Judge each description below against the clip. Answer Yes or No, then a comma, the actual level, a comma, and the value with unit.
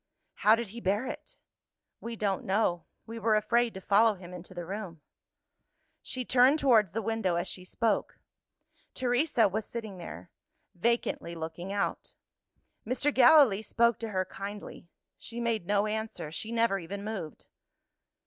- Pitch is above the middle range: Yes, high, 215 Hz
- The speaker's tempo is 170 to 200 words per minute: No, average, 150 wpm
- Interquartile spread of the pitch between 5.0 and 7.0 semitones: No, average, 3.7 semitones